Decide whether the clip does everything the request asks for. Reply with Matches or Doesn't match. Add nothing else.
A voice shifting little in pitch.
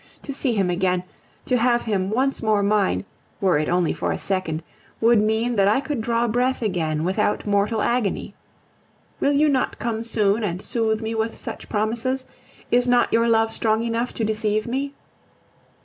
Doesn't match